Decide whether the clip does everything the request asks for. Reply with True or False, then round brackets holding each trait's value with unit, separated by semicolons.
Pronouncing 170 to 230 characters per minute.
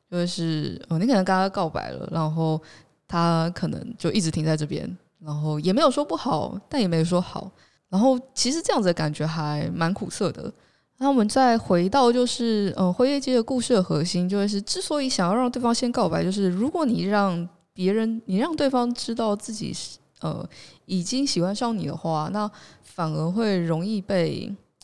False (285 characters per minute)